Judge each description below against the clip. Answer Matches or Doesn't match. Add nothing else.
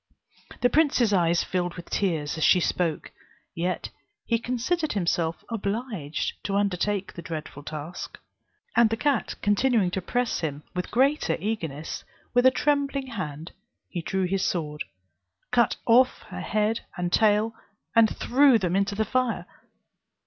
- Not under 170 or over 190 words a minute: Doesn't match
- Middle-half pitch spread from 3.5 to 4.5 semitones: Doesn't match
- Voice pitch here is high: Matches